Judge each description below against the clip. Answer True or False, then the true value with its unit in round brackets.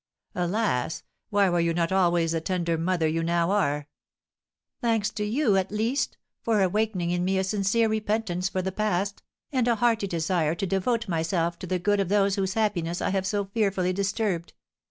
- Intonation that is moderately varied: True (3.4 semitones)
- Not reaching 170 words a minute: False (185 wpm)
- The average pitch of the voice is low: False (190 Hz)